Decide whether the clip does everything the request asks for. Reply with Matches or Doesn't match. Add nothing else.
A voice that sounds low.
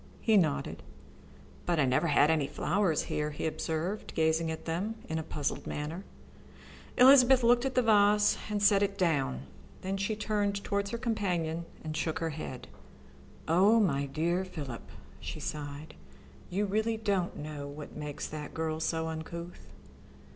Doesn't match